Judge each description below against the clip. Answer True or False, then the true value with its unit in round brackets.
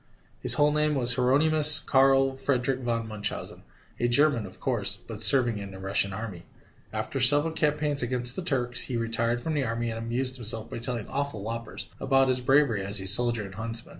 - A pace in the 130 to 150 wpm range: False (195 wpm)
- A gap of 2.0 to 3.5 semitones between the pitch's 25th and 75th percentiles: True (3.1 semitones)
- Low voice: True (120 Hz)